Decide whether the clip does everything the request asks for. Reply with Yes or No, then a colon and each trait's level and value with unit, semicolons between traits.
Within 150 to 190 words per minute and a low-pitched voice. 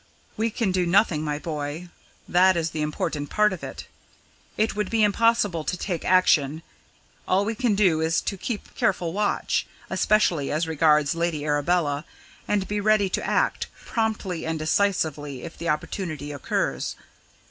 No: average, 160 wpm; medium, 175 Hz